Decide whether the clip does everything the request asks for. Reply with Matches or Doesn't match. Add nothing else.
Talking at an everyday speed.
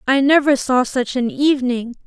Matches